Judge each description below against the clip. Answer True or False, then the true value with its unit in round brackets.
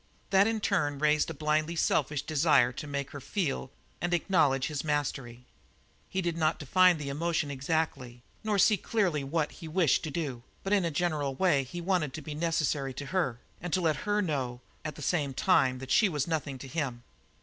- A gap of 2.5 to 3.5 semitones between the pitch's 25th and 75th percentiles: False (3.9 semitones)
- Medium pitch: True (150 Hz)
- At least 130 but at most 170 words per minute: False (200 wpm)